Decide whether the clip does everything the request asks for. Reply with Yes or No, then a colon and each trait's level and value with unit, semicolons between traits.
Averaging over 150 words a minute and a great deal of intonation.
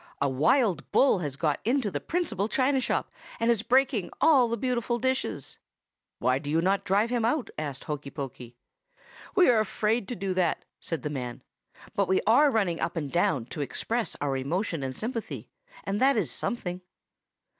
Yes: average, 180 wpm; wide, 8.2 semitones